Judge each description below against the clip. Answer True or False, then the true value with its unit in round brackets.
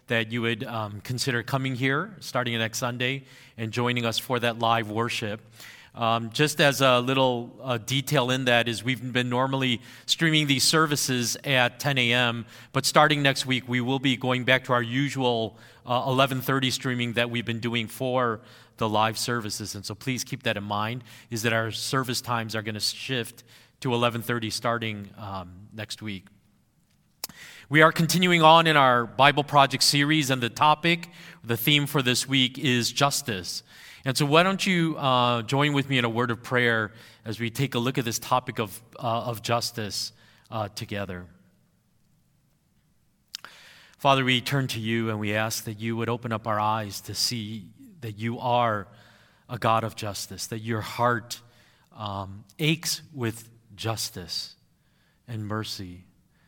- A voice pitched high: False (120 Hz)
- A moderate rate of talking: True (170 wpm)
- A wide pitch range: False (2.9 semitones)